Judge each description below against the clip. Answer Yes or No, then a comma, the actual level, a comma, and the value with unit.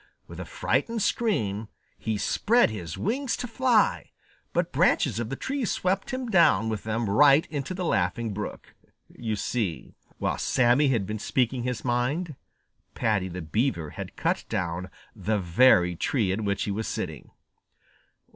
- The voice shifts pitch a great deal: Yes, wide, 8.4 semitones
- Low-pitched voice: Yes, low, 115 Hz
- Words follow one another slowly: No, average, 155 wpm